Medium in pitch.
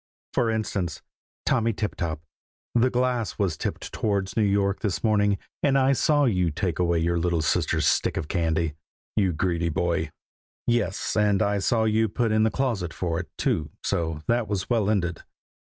No: low, 100 Hz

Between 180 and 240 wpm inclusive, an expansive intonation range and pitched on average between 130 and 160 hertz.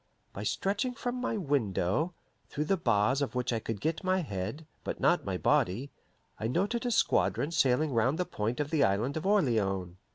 Yes: average, 190 wpm; wide, 8.5 semitones; medium, 140 Hz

